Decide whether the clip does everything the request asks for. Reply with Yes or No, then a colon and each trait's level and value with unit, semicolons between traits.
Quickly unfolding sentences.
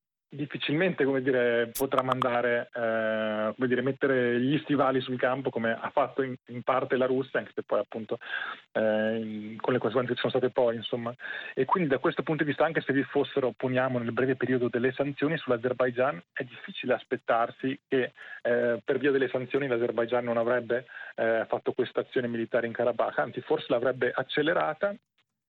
Yes: fast, 180 wpm